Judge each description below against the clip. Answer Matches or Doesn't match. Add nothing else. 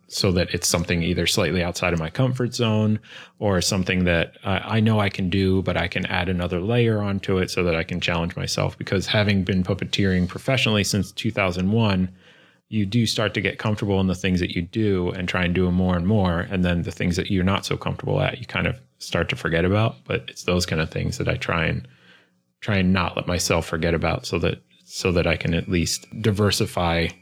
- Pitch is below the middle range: Matches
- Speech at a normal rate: Doesn't match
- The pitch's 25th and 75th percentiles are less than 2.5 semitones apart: Doesn't match